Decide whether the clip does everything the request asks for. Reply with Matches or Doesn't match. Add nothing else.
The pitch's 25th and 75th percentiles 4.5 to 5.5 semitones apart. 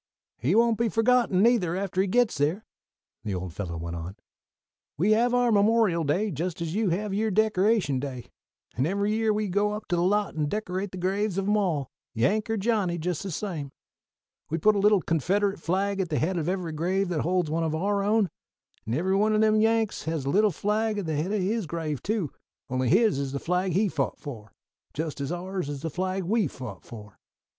Matches